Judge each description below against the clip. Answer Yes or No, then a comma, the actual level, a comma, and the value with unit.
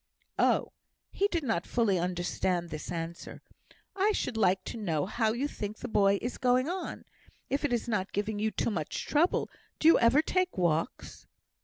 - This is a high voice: Yes, high, 220 Hz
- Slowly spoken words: No, average, 180 wpm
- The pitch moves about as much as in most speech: No, wide, 6.3 semitones